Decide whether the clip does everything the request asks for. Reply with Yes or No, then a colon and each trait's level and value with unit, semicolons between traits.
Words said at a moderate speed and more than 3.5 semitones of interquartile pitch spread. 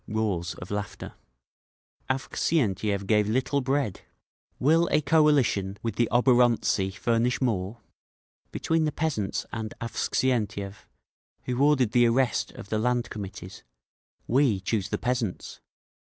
No: slow, 120 wpm; average, 4.3 semitones